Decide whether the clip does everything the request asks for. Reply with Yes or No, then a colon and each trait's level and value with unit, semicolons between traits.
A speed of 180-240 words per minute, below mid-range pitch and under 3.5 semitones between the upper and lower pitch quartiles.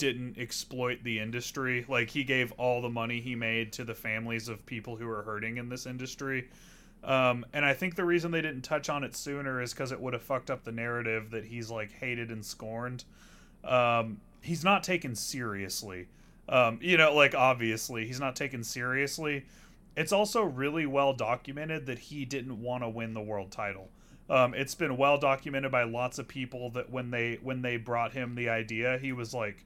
Yes: average, 200 wpm; low, 125 Hz; average, 2.9 semitones